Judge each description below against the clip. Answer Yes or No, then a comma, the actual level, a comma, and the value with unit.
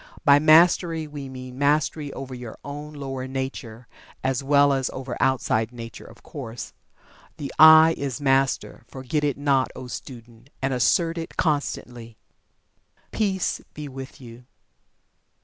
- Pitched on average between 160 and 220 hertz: No, low, 135 Hz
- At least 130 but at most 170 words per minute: Yes, slow, 135 wpm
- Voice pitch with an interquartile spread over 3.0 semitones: No, average, 2.7 semitones